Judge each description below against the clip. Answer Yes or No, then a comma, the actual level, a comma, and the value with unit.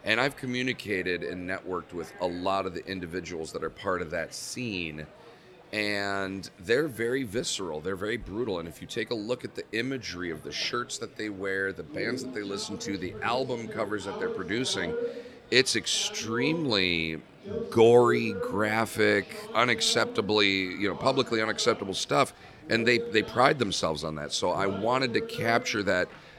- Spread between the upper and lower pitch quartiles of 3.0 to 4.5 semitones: No, average, 5.0 semitones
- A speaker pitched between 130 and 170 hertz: No, low, 105 Hz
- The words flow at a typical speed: Yes, average, 170 wpm